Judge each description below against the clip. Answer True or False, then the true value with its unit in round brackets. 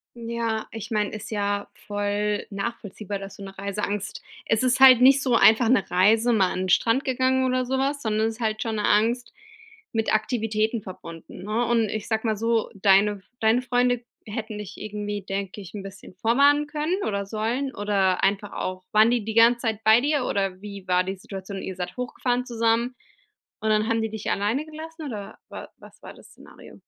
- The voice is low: False (220 Hz)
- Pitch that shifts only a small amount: False (3.1 semitones)